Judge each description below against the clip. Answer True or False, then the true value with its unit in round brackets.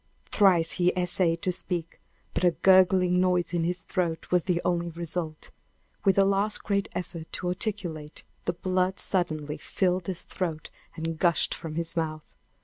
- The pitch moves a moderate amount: False (2.0 semitones)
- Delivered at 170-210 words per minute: False (160 wpm)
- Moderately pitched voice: True (180 Hz)